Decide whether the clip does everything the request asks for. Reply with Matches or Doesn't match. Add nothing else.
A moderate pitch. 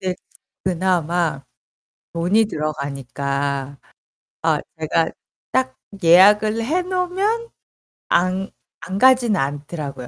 Matches